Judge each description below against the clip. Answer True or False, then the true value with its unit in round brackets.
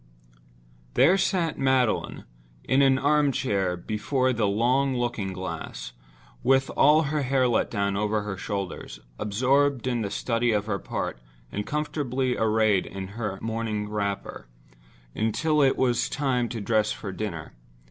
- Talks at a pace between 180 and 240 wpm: False (145 wpm)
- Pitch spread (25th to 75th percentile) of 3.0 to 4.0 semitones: False (4.4 semitones)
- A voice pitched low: True (115 Hz)